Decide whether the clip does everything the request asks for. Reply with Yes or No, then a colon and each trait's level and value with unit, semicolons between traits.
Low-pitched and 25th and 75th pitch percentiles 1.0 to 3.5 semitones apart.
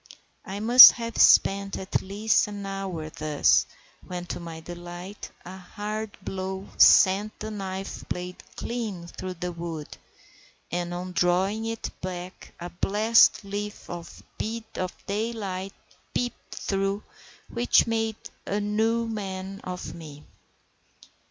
No: high, 195 Hz; average, 3.1 semitones